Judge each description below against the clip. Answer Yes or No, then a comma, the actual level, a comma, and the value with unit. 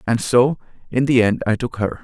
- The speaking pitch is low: Yes, low, 120 Hz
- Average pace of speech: No, fast, 235 wpm